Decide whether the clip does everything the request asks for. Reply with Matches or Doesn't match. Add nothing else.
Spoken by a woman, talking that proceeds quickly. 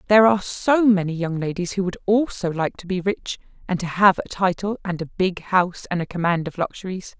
Matches